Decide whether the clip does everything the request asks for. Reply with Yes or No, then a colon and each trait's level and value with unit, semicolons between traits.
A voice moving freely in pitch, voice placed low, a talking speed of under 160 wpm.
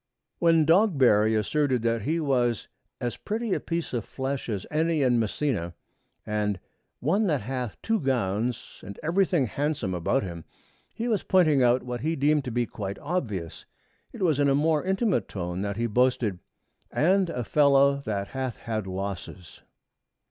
No: wide, 6.6 semitones; low, 130 Hz; average, 165 wpm